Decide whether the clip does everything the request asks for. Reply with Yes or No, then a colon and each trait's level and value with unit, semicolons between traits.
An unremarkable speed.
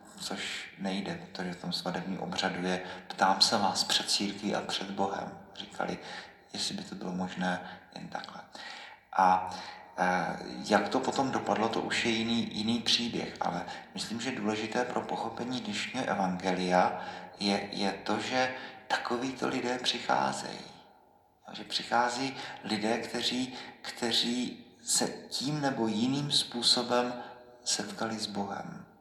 Yes: average, 130 wpm